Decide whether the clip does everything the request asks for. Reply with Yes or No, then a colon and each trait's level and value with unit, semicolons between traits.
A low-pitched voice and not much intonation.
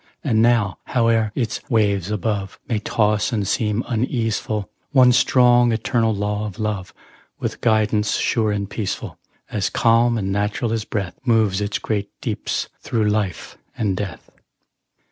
Yes: low, 110 Hz; narrow, 2.0 semitones